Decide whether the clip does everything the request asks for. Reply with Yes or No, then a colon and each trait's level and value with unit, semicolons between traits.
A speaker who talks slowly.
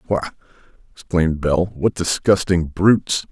Yes: slow, 110 wpm